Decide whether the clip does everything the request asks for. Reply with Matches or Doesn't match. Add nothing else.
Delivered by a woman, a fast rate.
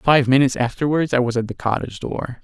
Doesn't match